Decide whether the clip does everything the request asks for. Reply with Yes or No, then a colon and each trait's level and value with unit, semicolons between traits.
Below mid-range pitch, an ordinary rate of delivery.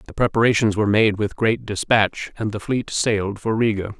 Yes: low, 105 Hz; average, 195 wpm